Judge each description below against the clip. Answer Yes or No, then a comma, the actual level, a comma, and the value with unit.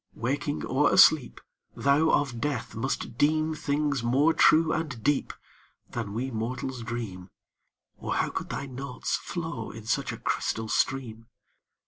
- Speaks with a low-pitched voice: Yes, low, 130 Hz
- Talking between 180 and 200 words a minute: No, average, 140 wpm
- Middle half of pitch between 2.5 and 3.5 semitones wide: No, average, 4.2 semitones